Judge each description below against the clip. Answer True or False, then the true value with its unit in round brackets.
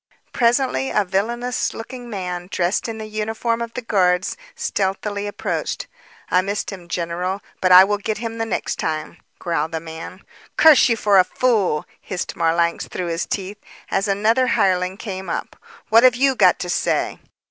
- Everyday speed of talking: True (170 wpm)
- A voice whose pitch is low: False (200 Hz)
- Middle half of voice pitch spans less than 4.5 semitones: True (4.0 semitones)